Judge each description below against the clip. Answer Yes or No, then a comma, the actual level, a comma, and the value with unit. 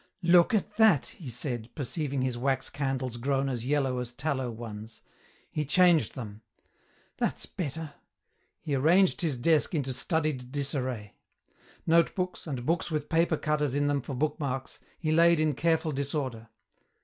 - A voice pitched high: No, medium, 140 Hz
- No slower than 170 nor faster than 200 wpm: No, average, 150 wpm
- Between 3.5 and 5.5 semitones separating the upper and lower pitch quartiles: Yes, average, 4.0 semitones